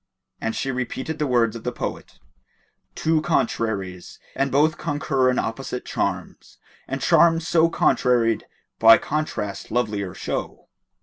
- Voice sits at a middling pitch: No, low, 130 Hz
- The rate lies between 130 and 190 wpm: Yes, slow, 135 wpm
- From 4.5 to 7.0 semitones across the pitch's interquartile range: Yes, average, 5.3 semitones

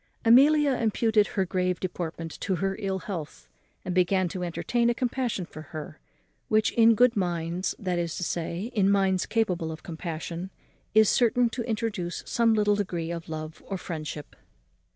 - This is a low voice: No, high, 190 Hz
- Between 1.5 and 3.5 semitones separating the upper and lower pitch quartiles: No, average, 4.6 semitones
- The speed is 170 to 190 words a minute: Yes, average, 175 wpm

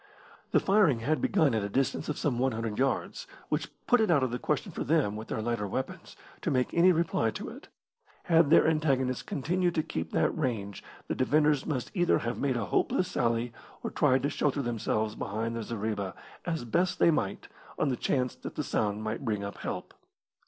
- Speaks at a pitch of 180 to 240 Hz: No, low, 130 Hz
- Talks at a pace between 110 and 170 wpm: No, average, 200 wpm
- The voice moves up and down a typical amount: No, wide, 5.8 semitones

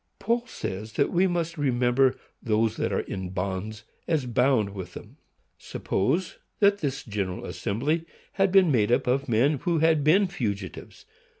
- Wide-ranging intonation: Yes, wide, 7.5 semitones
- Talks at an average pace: Yes, average, 160 wpm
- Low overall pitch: Yes, low, 130 Hz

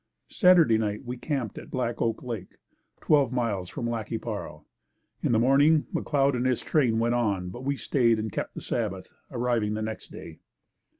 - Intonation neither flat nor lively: Yes, average, 3.2 semitones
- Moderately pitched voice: No, low, 120 Hz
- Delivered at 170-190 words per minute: Yes, average, 185 wpm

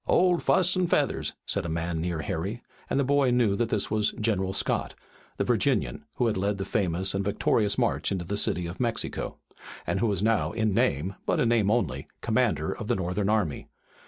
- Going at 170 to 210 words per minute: Yes, fast, 205 wpm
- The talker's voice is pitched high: No, low, 100 Hz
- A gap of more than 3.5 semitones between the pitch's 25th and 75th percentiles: Yes, average, 4.0 semitones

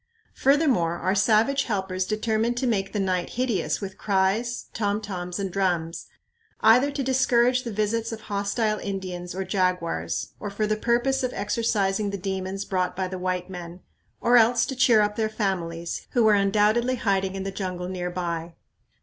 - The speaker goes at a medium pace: Yes, average, 175 wpm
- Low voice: No, high, 200 Hz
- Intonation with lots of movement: No, average, 3.7 semitones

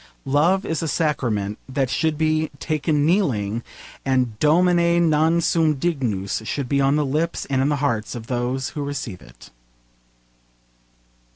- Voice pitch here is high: No, medium, 145 Hz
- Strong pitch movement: No, average, 4.3 semitones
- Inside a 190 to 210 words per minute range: No, average, 150 wpm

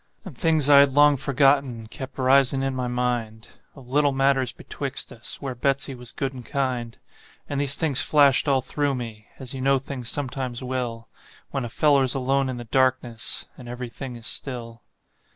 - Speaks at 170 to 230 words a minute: Yes, average, 185 wpm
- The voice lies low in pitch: Yes, low, 130 Hz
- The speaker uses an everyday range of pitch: No, narrow, 2.2 semitones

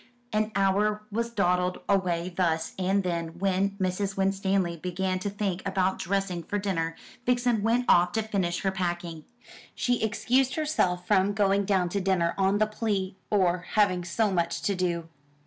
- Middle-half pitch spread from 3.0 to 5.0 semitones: No, narrow, 2.4 semitones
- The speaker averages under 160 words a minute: No, average, 165 wpm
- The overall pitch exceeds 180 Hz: Yes, high, 190 Hz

